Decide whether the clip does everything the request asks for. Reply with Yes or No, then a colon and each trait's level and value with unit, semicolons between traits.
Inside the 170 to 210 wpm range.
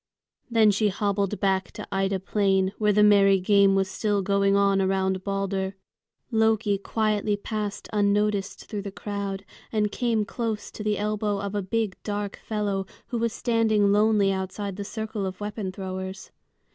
No: average, 160 wpm